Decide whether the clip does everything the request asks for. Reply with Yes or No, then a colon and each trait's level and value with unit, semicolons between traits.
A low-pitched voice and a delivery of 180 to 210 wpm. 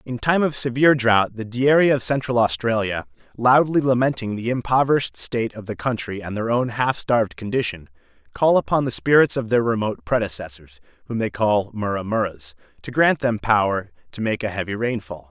Yes: low, 115 Hz; average, 185 wpm